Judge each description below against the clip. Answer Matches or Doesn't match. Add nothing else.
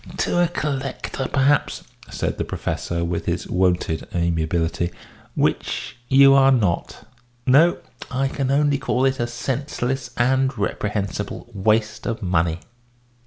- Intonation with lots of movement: Matches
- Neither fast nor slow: Doesn't match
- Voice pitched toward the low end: Matches